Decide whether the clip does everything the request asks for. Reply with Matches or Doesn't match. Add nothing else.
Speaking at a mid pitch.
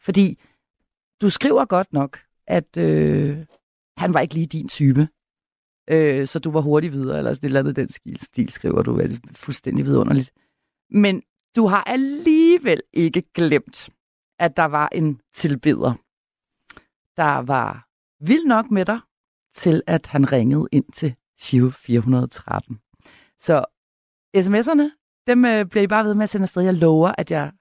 Matches